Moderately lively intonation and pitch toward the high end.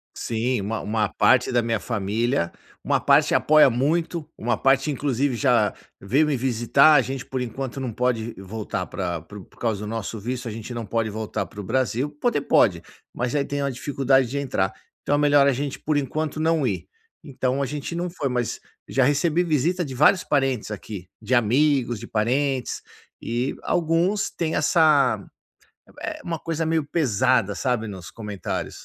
No: average, 4.4 semitones; low, 130 Hz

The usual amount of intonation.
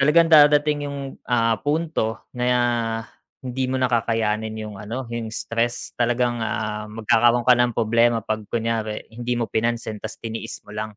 No: narrow, 1.9 semitones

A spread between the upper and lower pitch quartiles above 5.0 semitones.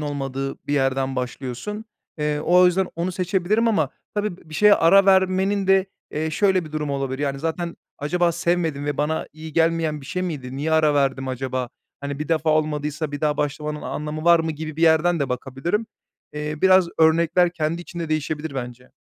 No: average, 3.4 semitones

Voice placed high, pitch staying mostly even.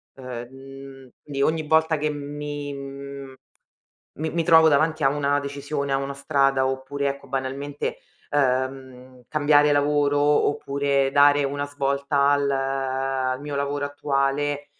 No: medium, 140 Hz; narrow, 1.1 semitones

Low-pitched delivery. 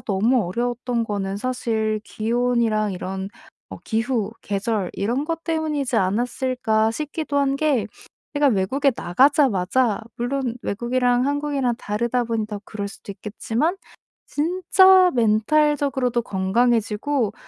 No: high, 240 Hz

